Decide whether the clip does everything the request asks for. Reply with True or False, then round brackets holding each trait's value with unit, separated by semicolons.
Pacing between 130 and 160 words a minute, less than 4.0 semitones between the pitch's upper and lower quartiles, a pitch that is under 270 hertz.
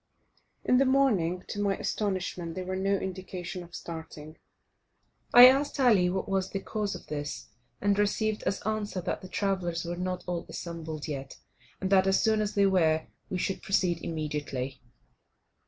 False (170 wpm; 3.2 semitones; 185 Hz)